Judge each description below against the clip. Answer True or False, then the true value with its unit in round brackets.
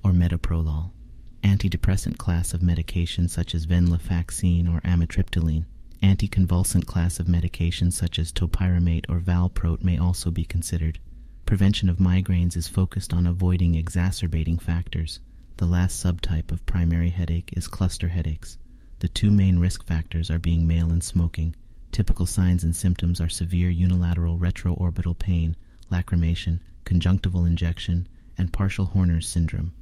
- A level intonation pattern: True (1.5 semitones)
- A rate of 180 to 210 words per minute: False (135 wpm)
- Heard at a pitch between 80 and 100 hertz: True (85 Hz)